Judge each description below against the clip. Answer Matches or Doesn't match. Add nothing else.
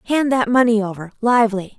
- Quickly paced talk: Doesn't match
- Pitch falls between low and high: Doesn't match